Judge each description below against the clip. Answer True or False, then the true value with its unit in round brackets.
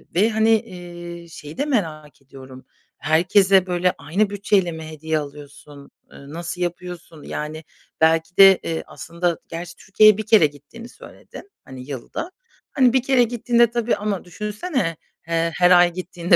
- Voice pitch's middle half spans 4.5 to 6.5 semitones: True (4.8 semitones)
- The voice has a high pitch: False (175 Hz)